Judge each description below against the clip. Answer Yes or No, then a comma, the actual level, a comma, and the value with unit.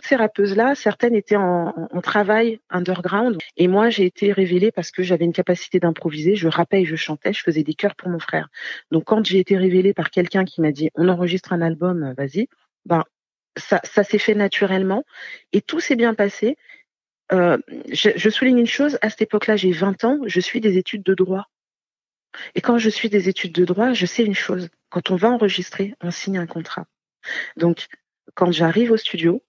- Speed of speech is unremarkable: Yes, average, 200 wpm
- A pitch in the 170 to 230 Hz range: Yes, high, 190 Hz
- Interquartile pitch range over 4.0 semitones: No, average, 3.4 semitones